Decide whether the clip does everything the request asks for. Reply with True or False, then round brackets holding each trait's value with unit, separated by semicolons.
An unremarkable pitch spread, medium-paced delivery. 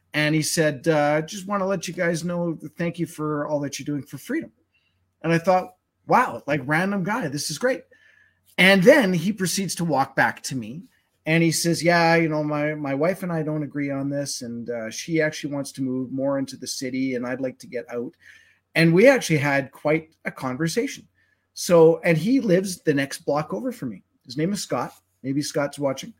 False (4.1 semitones; 220 wpm)